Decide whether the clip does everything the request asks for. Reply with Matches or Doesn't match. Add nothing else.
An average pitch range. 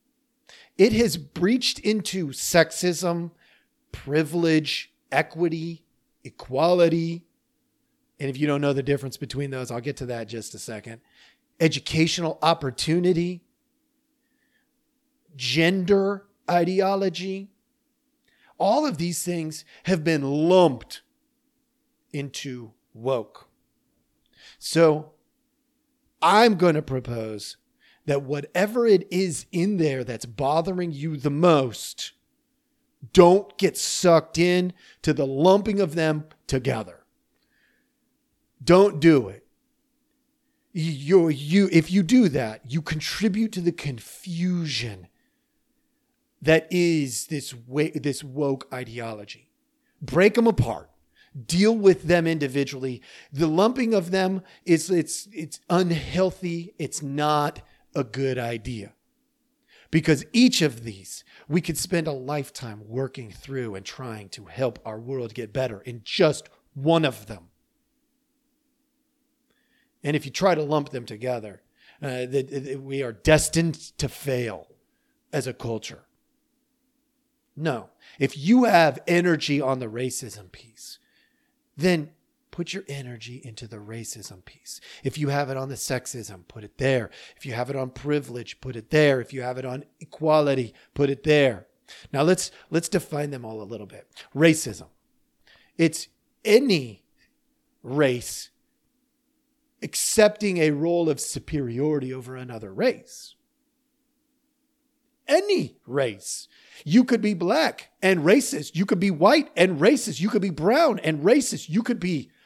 Doesn't match